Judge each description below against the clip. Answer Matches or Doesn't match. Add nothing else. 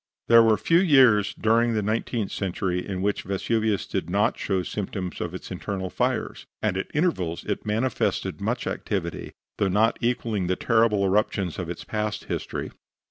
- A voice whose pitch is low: Matches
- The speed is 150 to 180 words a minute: Matches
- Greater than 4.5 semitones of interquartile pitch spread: Doesn't match